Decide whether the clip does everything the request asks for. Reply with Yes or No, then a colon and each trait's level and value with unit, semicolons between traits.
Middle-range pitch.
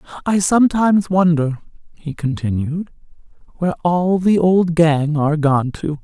Yes: medium, 165 Hz